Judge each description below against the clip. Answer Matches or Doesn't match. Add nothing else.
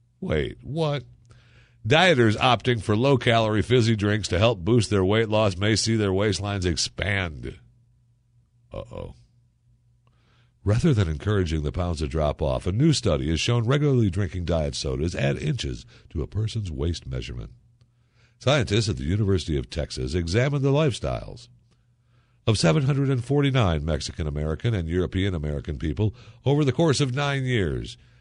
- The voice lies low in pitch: Matches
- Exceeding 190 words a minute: Doesn't match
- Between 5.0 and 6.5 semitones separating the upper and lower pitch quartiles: Matches